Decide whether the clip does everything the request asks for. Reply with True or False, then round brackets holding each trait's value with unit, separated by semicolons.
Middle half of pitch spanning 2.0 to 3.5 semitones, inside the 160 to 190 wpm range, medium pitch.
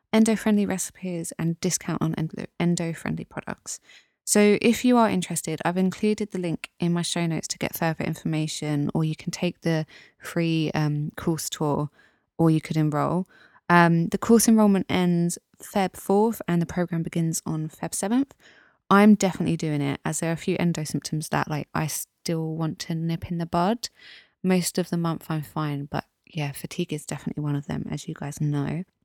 True (3.0 semitones; 185 wpm; 170 Hz)